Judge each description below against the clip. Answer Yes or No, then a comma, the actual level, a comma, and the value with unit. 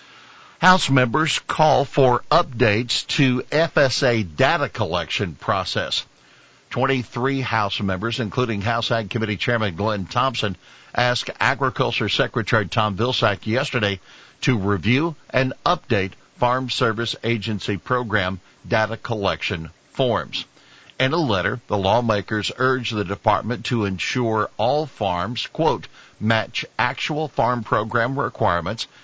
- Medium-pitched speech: No, low, 120 Hz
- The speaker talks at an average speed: No, slow, 115 wpm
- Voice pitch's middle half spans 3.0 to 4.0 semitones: Yes, average, 3.4 semitones